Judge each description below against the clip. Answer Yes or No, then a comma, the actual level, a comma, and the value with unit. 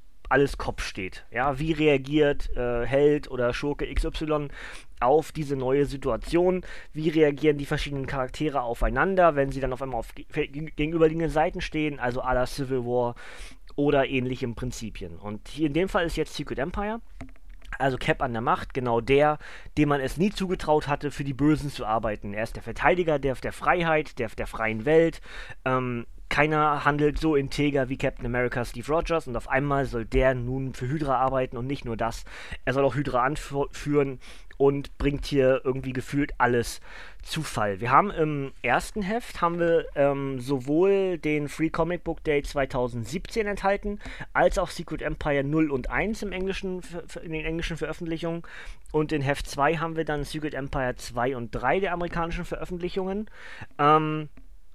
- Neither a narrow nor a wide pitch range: Yes, average, 3.6 semitones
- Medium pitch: Yes, medium, 145 Hz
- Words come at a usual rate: Yes, average, 170 wpm